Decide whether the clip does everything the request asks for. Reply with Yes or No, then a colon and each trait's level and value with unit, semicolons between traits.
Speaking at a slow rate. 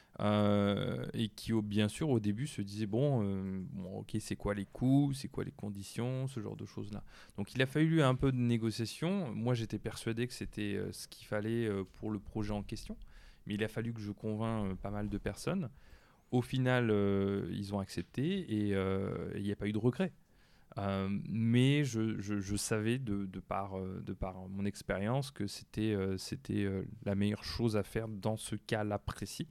No: average, 210 wpm